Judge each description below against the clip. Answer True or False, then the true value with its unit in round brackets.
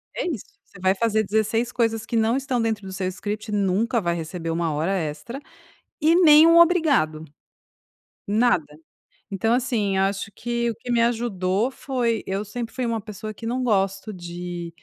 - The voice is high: True (220 Hz)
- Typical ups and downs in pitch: True (4.0 semitones)